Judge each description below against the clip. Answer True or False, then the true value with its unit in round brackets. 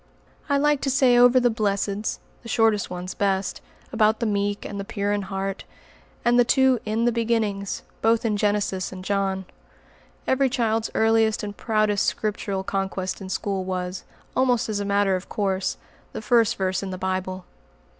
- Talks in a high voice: True (205 Hz)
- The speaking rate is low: False (175 wpm)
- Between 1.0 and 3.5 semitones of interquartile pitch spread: True (2.9 semitones)